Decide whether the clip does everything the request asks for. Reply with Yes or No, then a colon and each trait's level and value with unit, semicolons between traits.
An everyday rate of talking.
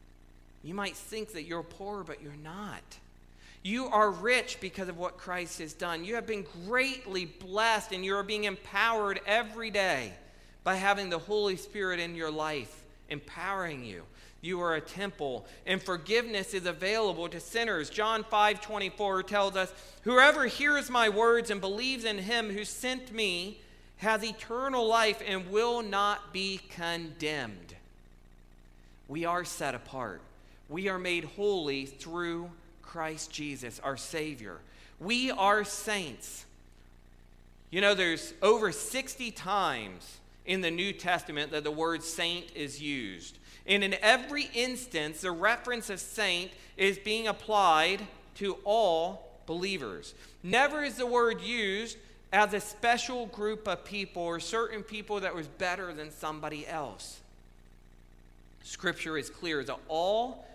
Yes: average, 145 wpm